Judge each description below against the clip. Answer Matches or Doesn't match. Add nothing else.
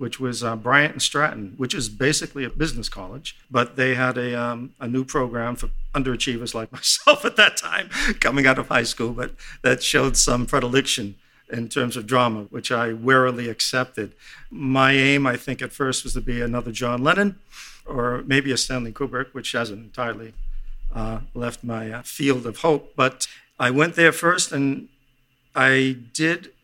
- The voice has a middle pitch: Doesn't match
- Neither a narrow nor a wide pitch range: Doesn't match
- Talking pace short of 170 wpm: Doesn't match